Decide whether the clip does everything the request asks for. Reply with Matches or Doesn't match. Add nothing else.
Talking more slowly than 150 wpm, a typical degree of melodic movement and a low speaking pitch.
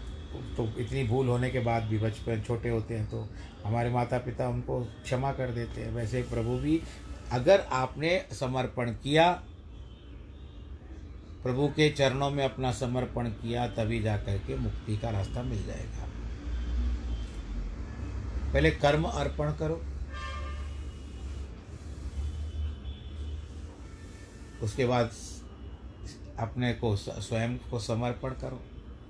Doesn't match